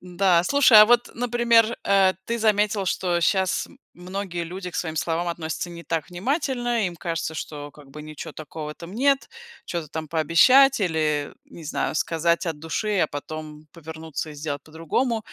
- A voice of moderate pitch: Yes, medium, 170 Hz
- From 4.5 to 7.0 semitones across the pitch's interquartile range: Yes, average, 5.1 semitones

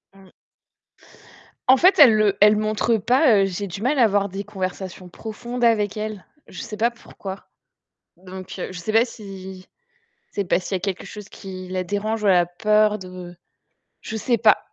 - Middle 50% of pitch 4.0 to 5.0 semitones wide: No, average, 2.8 semitones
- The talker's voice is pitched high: Yes, high, 205 Hz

